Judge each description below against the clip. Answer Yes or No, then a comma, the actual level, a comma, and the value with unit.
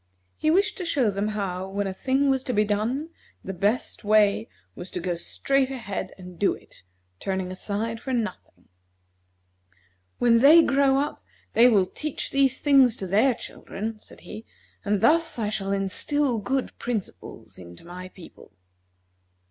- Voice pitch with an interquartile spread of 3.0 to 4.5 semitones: No, wide, 5.6 semitones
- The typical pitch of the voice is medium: No, high, 215 Hz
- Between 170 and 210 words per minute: No, average, 160 wpm